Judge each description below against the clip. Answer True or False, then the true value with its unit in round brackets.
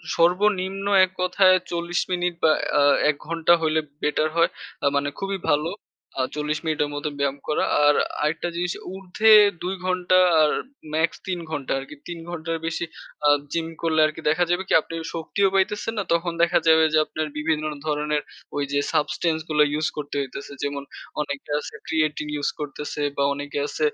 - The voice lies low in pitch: False (160 Hz)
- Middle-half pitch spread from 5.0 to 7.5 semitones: False (2.9 semitones)